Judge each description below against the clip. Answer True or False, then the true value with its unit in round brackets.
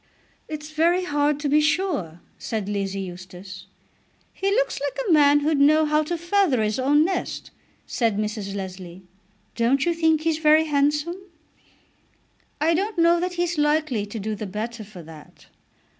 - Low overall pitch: False (290 Hz)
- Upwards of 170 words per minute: False (160 wpm)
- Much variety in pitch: True (7.4 semitones)